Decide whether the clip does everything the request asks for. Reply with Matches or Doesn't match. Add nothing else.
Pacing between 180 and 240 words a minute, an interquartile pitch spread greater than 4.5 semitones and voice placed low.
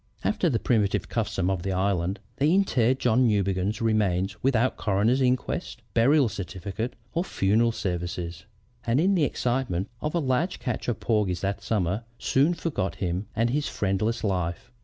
Doesn't match